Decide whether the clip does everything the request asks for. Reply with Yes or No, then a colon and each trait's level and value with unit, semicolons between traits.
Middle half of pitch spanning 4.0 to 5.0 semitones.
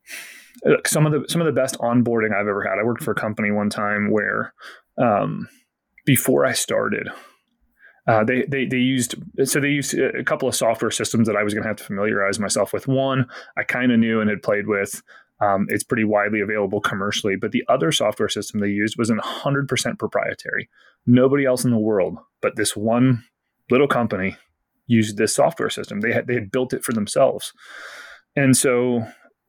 No: average, 3.5 semitones